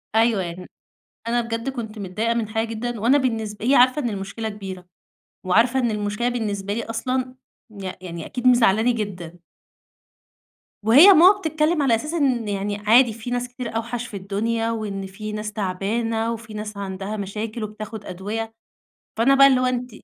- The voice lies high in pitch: Yes, high, 225 Hz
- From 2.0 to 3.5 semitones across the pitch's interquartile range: Yes, average, 2.9 semitones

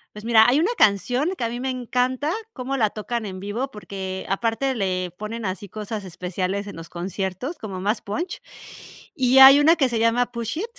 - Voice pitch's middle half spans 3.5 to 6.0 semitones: Yes, average, 4.6 semitones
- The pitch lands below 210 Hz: No, high, 225 Hz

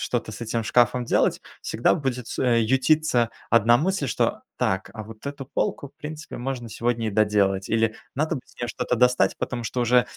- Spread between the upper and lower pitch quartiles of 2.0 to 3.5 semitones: Yes, average, 2.9 semitones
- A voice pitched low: Yes, low, 120 Hz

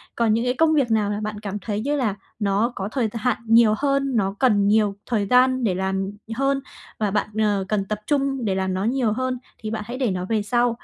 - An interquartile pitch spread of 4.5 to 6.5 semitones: No, average, 3.8 semitones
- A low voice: No, high, 220 Hz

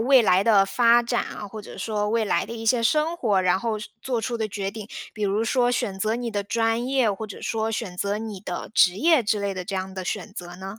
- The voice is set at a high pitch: Yes, high, 215 Hz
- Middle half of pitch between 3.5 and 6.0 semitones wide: No, average, 3.0 semitones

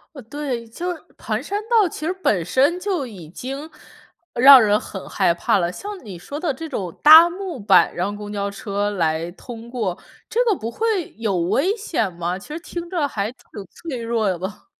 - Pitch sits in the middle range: No, high, 235 Hz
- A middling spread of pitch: No, wide, 8.6 semitones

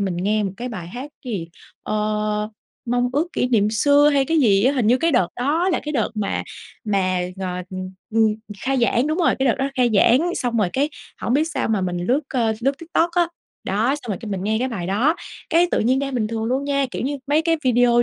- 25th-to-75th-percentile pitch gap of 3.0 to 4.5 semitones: No, average, 4.9 semitones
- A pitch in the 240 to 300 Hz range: Yes, high, 245 Hz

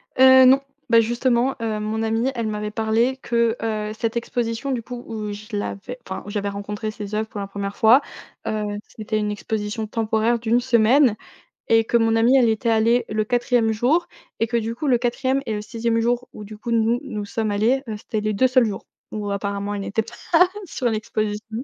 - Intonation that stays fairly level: Yes, narrow, 2.1 semitones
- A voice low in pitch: No, high, 225 Hz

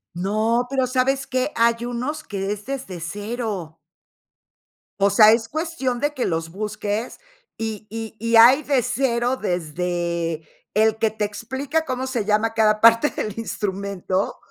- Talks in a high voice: Yes, high, 225 Hz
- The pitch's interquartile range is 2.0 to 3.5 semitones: No, average, 3.9 semitones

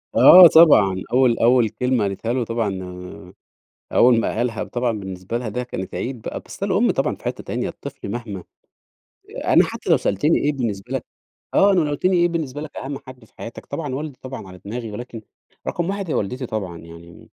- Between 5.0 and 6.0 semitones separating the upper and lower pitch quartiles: Yes, average, 5.3 semitones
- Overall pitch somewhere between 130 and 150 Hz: No, low, 120 Hz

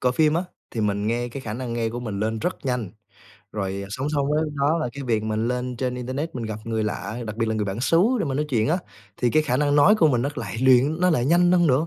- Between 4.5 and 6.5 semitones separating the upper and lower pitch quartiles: Yes, average, 4.8 semitones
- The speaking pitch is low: Yes, low, 125 Hz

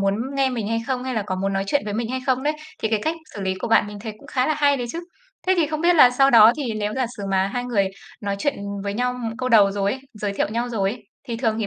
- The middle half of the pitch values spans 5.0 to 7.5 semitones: No, average, 4.2 semitones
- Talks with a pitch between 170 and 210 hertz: No, high, 230 Hz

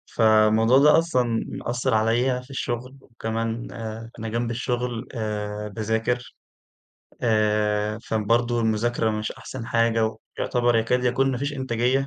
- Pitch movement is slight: Yes, narrow, 2.0 semitones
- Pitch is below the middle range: Yes, low, 115 Hz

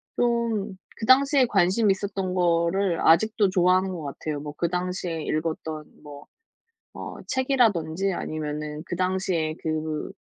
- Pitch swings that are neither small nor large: Yes, average, 4.1 semitones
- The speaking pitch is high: No, medium, 180 Hz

